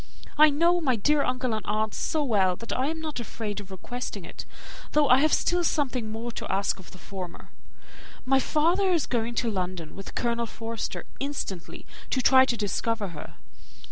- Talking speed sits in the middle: Yes, average, 185 wpm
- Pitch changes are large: Yes, wide, 5.7 semitones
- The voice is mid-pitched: No, high, 235 Hz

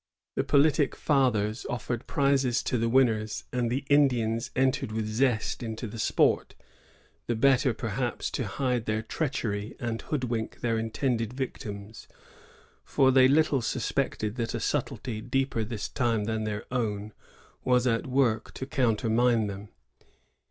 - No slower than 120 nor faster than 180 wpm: Yes, average, 140 wpm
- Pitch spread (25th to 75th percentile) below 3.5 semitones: Yes, average, 3.1 semitones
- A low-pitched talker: Yes, low, 120 Hz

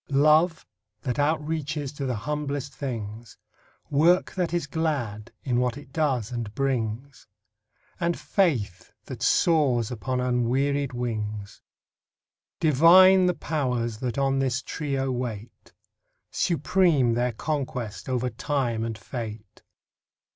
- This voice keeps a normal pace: No, slow, 115 wpm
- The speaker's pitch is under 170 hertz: Yes, low, 135 Hz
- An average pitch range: Yes, average, 4.2 semitones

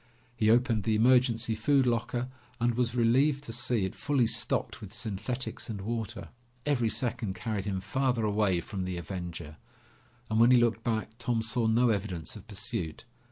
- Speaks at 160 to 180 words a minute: Yes, average, 170 wpm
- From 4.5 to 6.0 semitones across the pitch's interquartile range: No, average, 3.1 semitones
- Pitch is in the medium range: No, low, 115 Hz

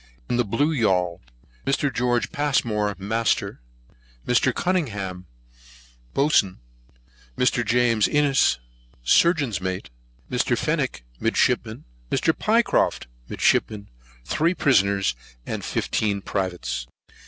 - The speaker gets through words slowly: Yes, slow, 90 wpm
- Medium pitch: No, low, 115 Hz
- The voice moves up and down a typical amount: No, wide, 6.4 semitones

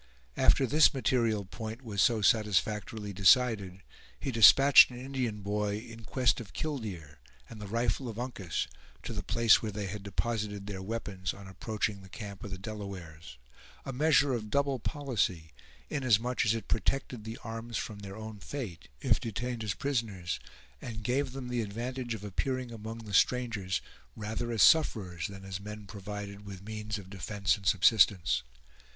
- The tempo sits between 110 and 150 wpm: No, average, 165 wpm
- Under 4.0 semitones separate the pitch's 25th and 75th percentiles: Yes, average, 3.3 semitones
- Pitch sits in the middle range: No, low, 110 Hz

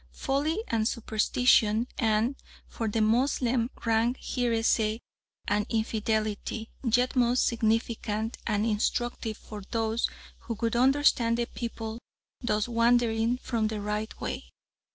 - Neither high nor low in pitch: No, high, 230 Hz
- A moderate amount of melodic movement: No, narrow, 1.8 semitones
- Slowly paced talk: Yes, slow, 115 wpm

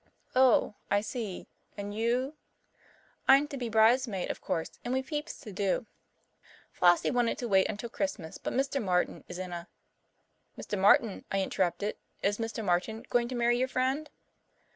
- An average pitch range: Yes, average, 4.5 semitones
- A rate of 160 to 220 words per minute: Yes, average, 170 wpm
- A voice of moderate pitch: No, high, 225 Hz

